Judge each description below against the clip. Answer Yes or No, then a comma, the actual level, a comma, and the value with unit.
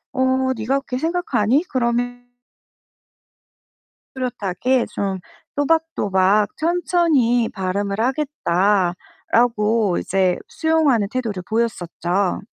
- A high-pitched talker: Yes, high, 235 Hz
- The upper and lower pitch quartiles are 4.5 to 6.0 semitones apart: Yes, average, 5.3 semitones